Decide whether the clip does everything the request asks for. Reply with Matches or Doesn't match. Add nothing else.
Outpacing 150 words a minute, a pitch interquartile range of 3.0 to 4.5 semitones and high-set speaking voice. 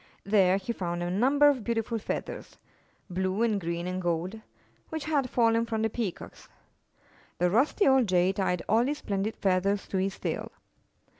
Matches